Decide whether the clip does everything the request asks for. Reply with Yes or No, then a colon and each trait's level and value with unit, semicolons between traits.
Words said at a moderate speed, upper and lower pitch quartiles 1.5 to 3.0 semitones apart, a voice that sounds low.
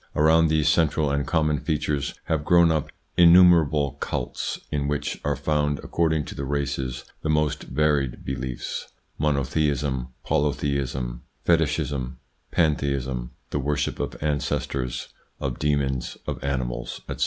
No: slow, 130 wpm; narrow, 2.4 semitones; very low, 70 Hz